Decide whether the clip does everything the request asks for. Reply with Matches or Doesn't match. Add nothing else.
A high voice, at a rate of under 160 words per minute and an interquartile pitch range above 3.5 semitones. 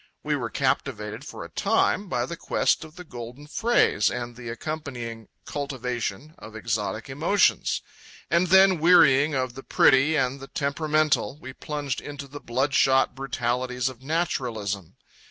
Doesn't match